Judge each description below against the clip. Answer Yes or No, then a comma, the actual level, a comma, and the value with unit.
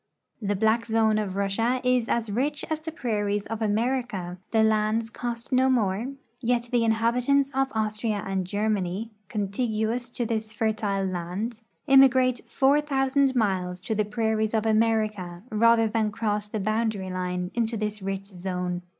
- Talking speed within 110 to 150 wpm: No, average, 160 wpm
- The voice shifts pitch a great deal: No, average, 2.8 semitones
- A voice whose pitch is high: Yes, high, 220 Hz